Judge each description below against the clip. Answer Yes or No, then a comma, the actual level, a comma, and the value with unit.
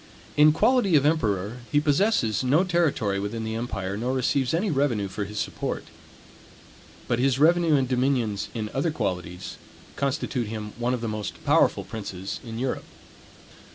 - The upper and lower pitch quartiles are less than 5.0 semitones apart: No, wide, 5.6 semitones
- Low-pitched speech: Yes, low, 125 Hz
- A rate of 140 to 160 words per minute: Yes, average, 155 wpm